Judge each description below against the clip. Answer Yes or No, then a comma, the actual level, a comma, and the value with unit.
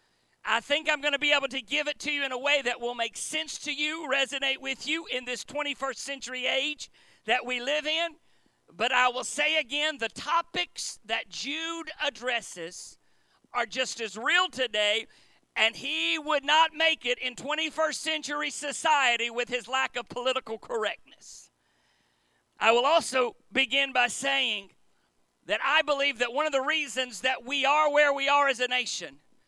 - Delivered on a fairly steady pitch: No, average, 3.4 semitones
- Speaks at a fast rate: No, average, 175 wpm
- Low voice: No, very high, 270 Hz